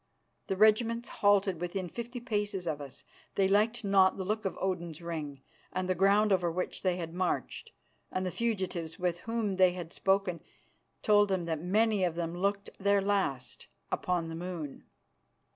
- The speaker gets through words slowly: No, average, 170 wpm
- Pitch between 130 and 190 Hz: Yes, medium, 185 Hz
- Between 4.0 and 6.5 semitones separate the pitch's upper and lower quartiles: No, average, 3.0 semitones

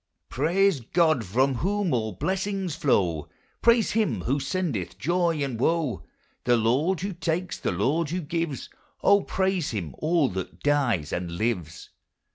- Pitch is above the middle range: No, medium, 145 Hz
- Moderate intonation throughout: No, wide, 7.7 semitones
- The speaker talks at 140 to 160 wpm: Yes, average, 145 wpm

